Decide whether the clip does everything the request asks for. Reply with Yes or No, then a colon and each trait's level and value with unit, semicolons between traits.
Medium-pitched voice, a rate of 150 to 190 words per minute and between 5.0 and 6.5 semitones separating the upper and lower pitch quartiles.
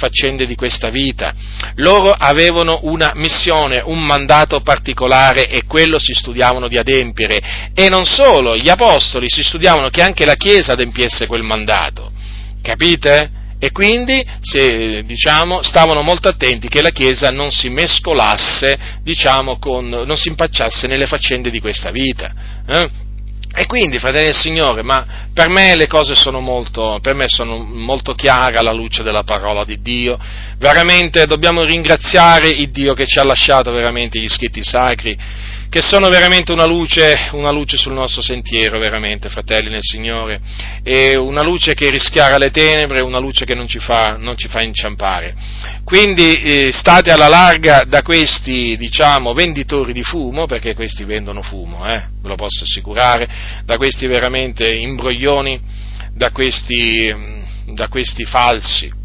No: low, 125 Hz; average, 155 wpm; average, 5.3 semitones